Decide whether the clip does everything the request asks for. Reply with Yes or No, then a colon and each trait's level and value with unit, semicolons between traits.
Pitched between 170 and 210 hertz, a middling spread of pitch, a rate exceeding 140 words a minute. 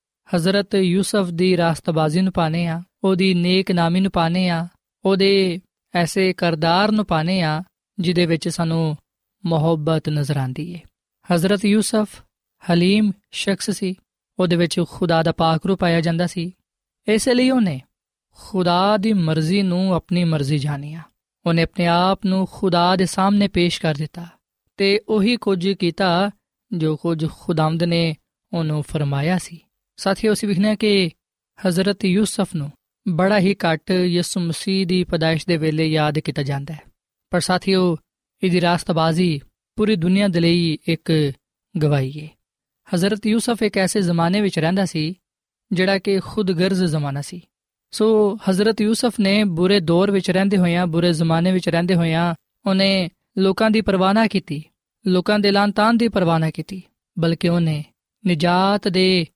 Yes: medium, 180 Hz; average, 3.0 semitones; average, 150 wpm